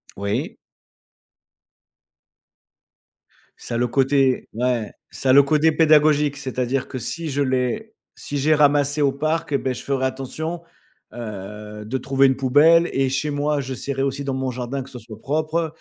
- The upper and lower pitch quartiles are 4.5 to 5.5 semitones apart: No, average, 2.7 semitones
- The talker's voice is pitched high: No, low, 135 Hz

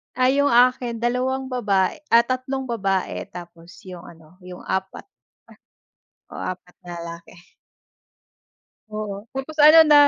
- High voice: Yes, high, 220 Hz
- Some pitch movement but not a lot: No, wide, 5.9 semitones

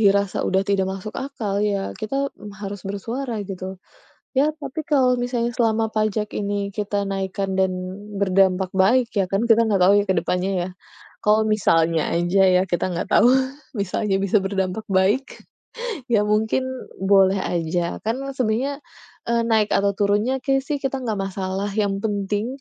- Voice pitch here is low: No, high, 205 Hz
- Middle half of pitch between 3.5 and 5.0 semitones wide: No, average, 3.1 semitones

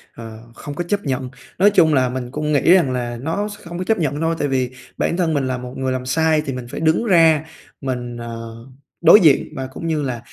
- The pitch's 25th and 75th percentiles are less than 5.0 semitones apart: Yes, average, 4.4 semitones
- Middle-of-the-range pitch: Yes, medium, 145 Hz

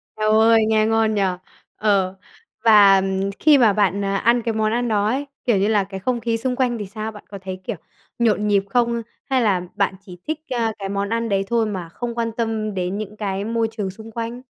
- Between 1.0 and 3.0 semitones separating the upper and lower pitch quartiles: Yes, narrow, 2.6 semitones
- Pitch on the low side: No, high, 215 Hz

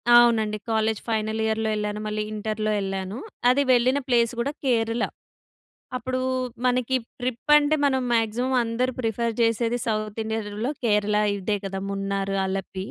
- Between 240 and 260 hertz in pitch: No, high, 225 Hz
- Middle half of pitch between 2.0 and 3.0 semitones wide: Yes, narrow, 2.5 semitones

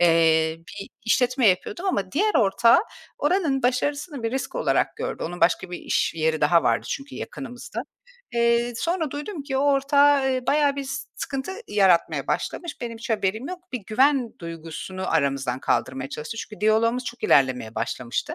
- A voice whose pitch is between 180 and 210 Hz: No, high, 235 Hz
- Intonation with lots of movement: Yes, wide, 8.1 semitones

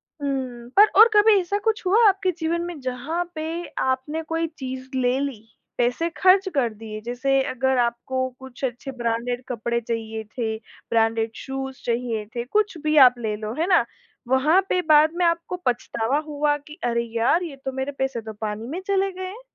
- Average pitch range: No, wide, 5.8 semitones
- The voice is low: No, very high, 265 Hz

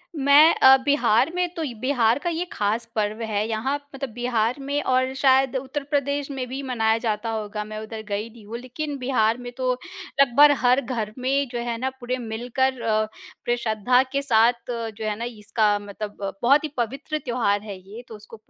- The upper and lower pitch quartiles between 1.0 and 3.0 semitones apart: No, average, 3.5 semitones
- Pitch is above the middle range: Yes, high, 240 Hz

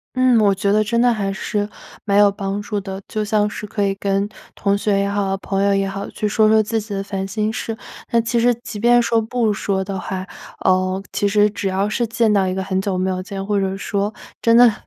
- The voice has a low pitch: No, high, 205 Hz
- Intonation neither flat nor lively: No, narrow, 2.0 semitones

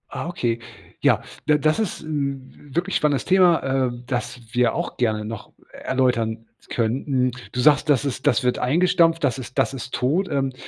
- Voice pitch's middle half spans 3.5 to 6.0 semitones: Yes, average, 3.8 semitones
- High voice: No, low, 135 Hz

